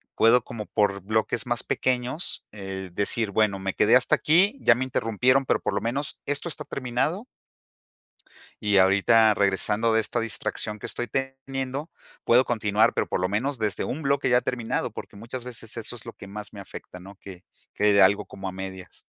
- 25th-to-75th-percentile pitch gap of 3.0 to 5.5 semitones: Yes, average, 4.0 semitones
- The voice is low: Yes, low, 115 Hz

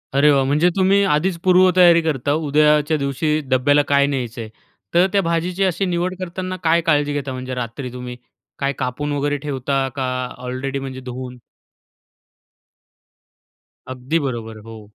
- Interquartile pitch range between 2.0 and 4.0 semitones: No, average, 4.5 semitones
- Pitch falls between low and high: Yes, medium, 145 Hz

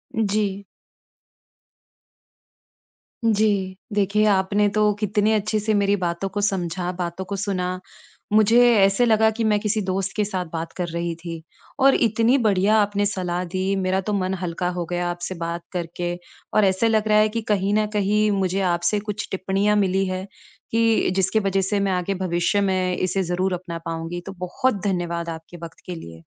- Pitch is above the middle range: Yes, high, 195 Hz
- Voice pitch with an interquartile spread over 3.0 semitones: No, average, 2.7 semitones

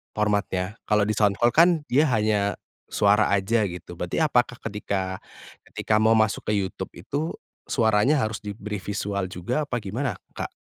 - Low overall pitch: Yes, low, 105 Hz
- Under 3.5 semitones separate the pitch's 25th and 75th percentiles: Yes, average, 2.7 semitones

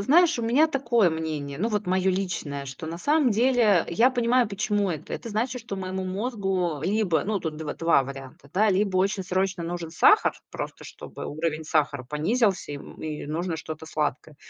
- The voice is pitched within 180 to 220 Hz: Yes, medium, 185 Hz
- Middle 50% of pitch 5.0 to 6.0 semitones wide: Yes, wide, 5.6 semitones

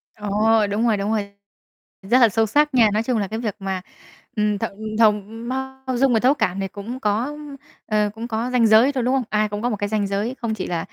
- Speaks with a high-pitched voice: Yes, high, 220 Hz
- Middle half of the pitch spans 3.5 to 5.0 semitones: No, average, 3.0 semitones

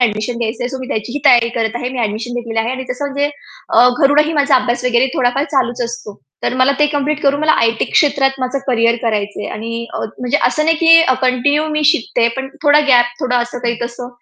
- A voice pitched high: Yes, very high, 250 Hz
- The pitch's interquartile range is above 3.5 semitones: No, average, 3.2 semitones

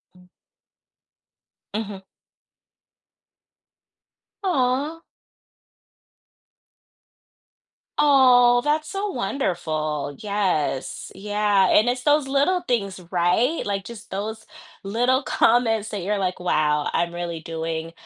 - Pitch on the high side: Yes, high, 210 Hz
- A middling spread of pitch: No, wide, 6.0 semitones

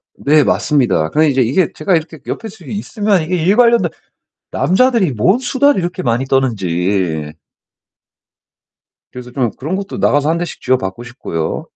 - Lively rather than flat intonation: Yes, wide, 7.9 semitones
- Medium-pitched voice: Yes, medium, 150 Hz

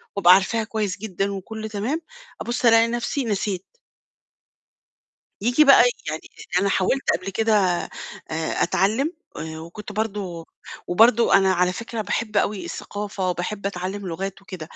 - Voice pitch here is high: Yes, high, 200 Hz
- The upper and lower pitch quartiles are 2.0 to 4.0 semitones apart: Yes, average, 3.3 semitones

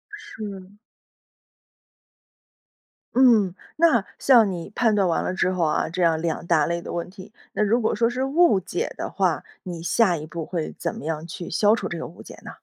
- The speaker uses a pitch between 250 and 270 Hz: No, medium, 185 Hz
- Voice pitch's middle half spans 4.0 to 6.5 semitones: Yes, average, 4.5 semitones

